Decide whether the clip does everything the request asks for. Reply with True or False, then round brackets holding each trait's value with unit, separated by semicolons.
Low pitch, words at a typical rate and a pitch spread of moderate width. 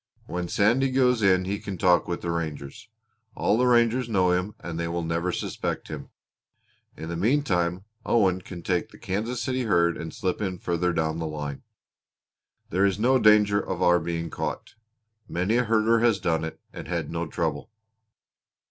True (90 Hz; 180 wpm; 4.5 semitones)